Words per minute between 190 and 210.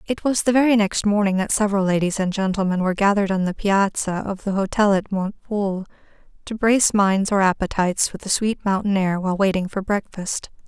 Yes: average, 195 wpm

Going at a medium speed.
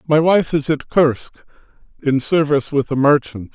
Yes: average, 170 wpm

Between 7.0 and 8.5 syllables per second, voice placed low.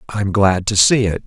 No: 4.6 syllables/s; low, 105 Hz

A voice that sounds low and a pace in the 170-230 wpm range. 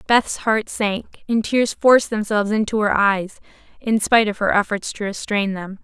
No: high, 210 Hz; average, 185 wpm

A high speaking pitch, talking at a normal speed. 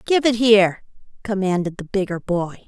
Yes: high, 200 Hz; average, 155 wpm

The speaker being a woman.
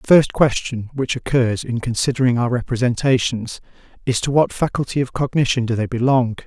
No: male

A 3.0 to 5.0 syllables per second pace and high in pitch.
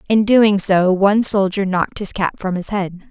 Yes: 4.8 syllables/s; high, 195 Hz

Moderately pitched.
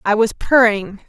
No: high, 215 Hz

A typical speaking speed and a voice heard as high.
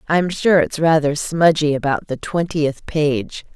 No: average, 150 wpm; medium, 155 Hz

